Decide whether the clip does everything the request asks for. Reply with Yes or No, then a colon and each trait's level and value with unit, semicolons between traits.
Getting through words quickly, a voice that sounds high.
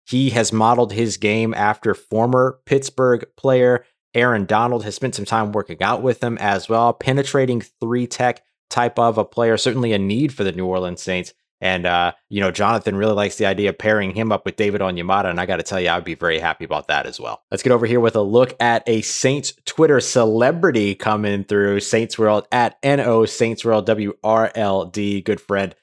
No: fast, 215 wpm; low, 110 Hz